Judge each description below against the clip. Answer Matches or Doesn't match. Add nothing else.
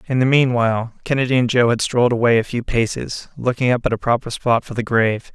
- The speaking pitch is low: Matches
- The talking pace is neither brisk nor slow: Doesn't match